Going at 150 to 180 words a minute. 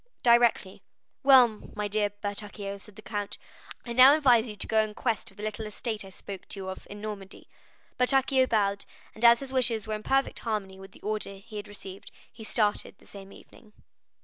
No: average, 200 wpm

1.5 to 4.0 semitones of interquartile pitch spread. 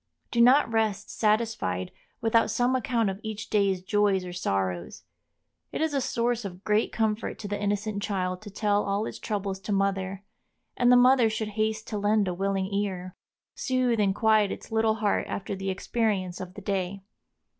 Yes: narrow, 2.5 semitones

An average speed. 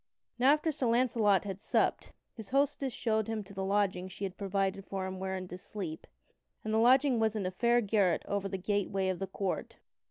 No: fast, 210 wpm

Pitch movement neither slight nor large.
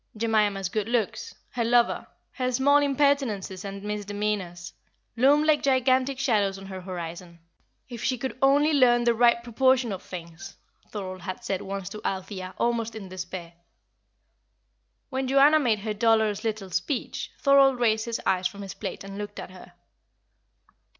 Yes: average, 4.8 semitones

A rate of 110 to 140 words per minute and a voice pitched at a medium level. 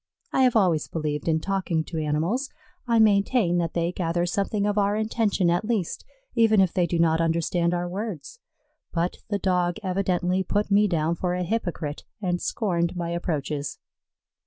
No: average, 170 wpm; medium, 180 Hz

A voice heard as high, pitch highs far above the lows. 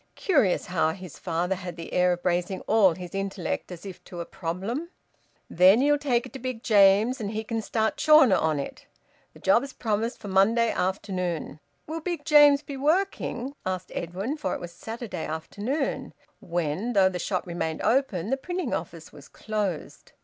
Yes: high, 200 Hz; wide, 6.1 semitones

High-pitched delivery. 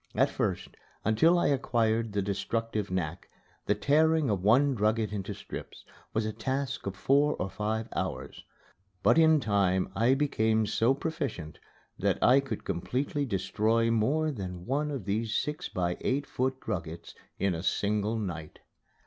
No: low, 110 Hz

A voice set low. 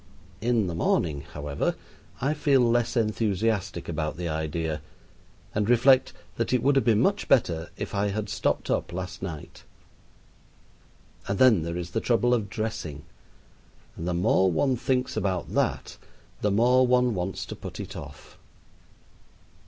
Yes: low, 105 Hz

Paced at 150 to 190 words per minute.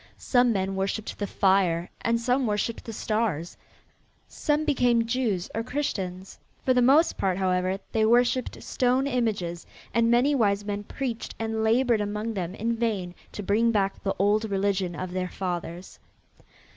Yes: average, 160 wpm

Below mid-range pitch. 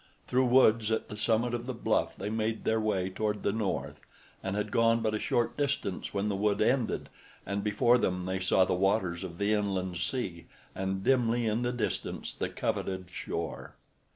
Yes: low, 105 Hz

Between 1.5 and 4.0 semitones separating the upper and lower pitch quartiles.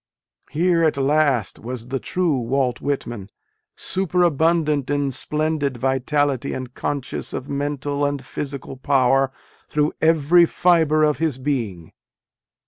Yes: average, 2.8 semitones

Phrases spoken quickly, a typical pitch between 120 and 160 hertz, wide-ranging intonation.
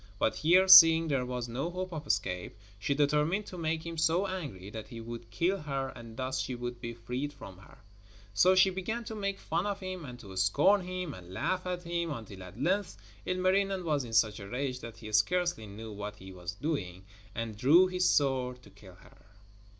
Yes: fast, 210 wpm; medium, 140 Hz; wide, 8.2 semitones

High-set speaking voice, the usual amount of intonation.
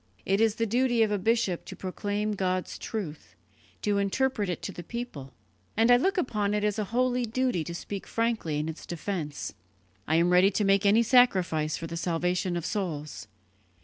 Yes: high, 200 Hz; average, 4.7 semitones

